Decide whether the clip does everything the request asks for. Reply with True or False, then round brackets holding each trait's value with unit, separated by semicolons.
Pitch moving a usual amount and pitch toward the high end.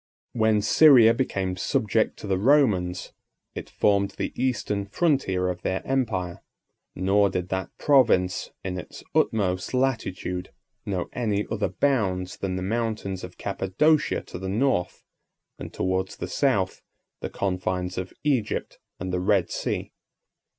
False (3.8 semitones; 100 Hz)